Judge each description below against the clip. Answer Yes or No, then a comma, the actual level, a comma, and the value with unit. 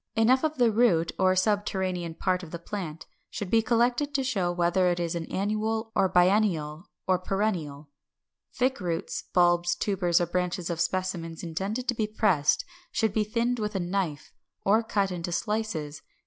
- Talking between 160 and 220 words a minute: Yes, average, 175 wpm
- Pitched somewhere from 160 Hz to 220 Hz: Yes, medium, 185 Hz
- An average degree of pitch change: Yes, average, 4.0 semitones